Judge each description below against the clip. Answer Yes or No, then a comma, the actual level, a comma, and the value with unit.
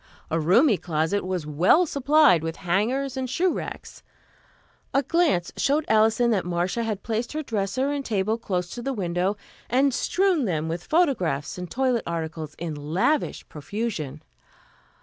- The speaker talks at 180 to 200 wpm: No, average, 150 wpm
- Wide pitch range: Yes, wide, 7.6 semitones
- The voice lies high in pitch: Yes, high, 210 Hz